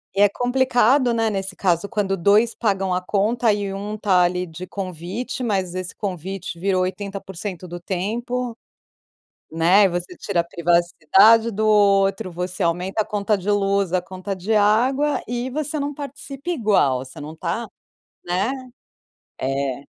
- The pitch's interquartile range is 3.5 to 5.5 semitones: Yes, average, 3.8 semitones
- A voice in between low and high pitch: No, high, 195 Hz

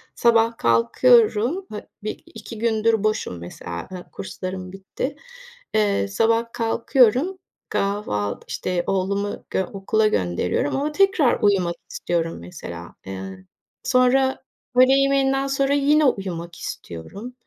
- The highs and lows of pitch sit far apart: Yes, wide, 6.2 semitones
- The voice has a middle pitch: No, high, 215 Hz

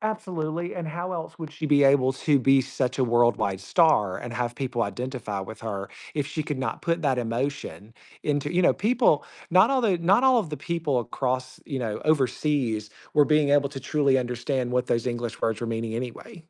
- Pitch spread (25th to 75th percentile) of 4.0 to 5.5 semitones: Yes, average, 4.8 semitones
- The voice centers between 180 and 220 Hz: No, low, 135 Hz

